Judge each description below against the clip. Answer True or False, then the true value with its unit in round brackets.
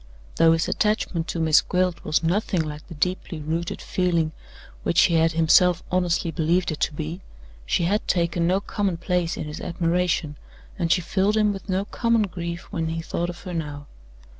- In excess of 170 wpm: True (190 wpm)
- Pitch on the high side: False (170 Hz)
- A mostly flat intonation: True (2.0 semitones)